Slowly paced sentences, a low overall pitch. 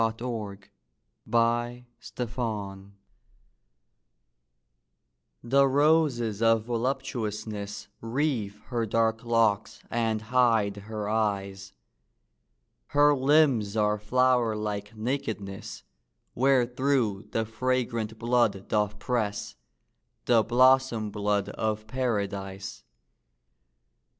Yes: slow, 80 wpm; low, 115 Hz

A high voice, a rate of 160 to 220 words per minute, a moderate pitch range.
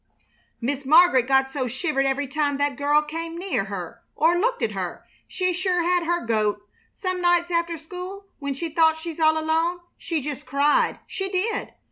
Yes: very high, 315 Hz; average, 185 wpm; average, 4.2 semitones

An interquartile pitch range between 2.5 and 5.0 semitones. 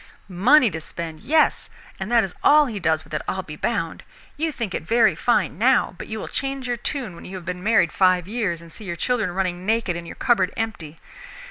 No: wide, 5.6 semitones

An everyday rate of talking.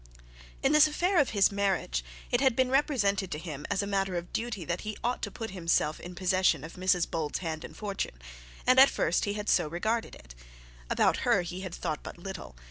No: fast, 215 wpm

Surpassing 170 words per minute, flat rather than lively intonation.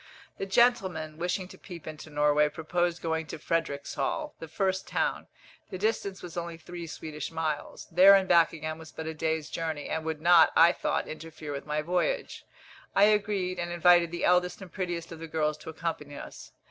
Yes: average, 190 wpm; narrow, 2.3 semitones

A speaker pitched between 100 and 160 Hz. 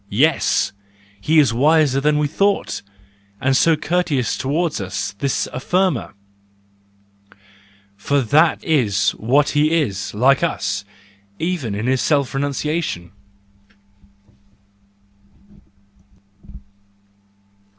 Yes: medium, 140 Hz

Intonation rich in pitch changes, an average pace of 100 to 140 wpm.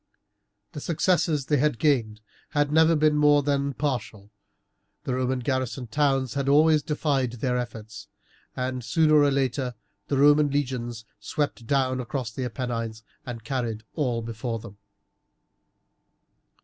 No: average, 3.6 semitones; slow, 135 wpm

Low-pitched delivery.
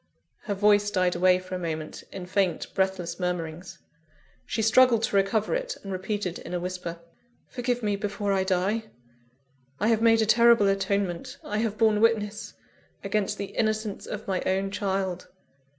No: high, 200 Hz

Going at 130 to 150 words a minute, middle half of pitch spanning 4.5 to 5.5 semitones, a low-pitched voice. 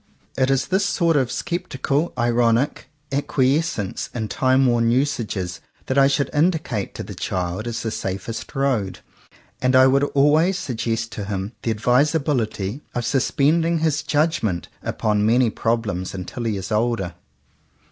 Yes: average, 145 wpm; average, 4.8 semitones; low, 125 Hz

